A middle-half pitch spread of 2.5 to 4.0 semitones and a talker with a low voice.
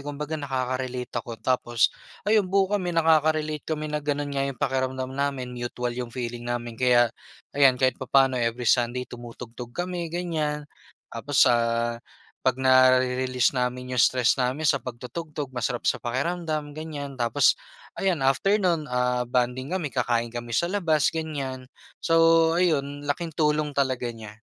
Yes: average, 3.7 semitones; low, 130 Hz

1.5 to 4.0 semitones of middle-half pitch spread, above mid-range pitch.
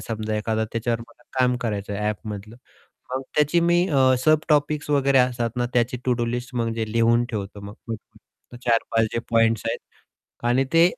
No: average, 2.8 semitones; low, 120 Hz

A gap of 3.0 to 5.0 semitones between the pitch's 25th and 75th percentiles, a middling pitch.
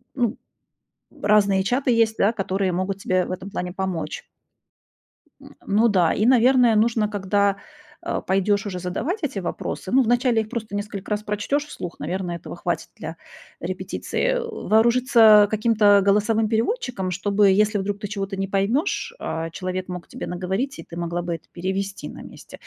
No: average, 3.3 semitones; high, 205 Hz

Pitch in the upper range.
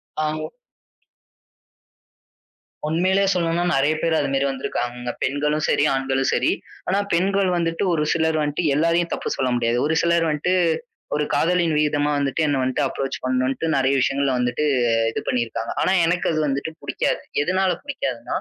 No: medium, 150 Hz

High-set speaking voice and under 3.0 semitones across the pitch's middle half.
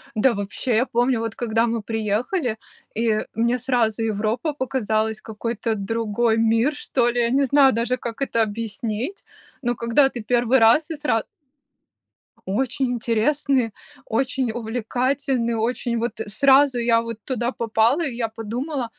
Yes: high, 235 Hz; narrow, 2.6 semitones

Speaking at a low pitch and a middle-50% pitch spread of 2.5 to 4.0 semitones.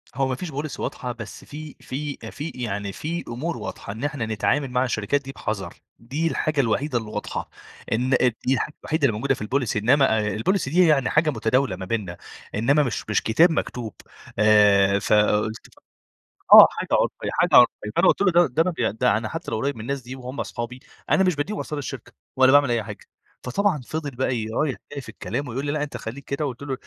No: low, 130 Hz; average, 4.6 semitones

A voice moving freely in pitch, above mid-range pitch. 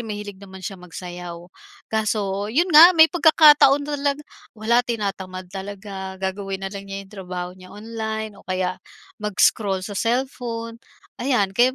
No: average, 3.7 semitones; high, 205 Hz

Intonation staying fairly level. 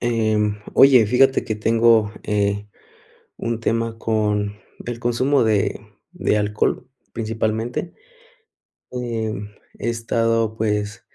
Yes: narrow, 1.8 semitones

